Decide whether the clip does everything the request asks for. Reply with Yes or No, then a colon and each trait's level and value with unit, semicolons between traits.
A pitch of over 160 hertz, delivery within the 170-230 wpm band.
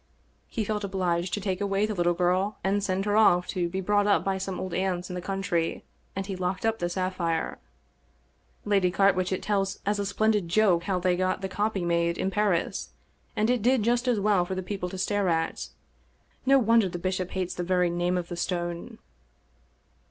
Yes: high, 190 Hz; fast, 205 wpm